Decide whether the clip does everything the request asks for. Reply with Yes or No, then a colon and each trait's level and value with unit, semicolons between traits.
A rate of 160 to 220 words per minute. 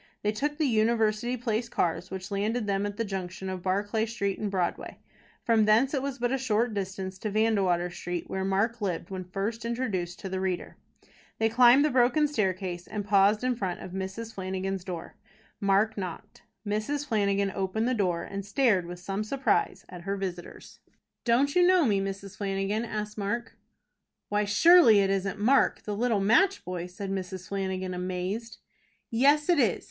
Yes: average, 180 wpm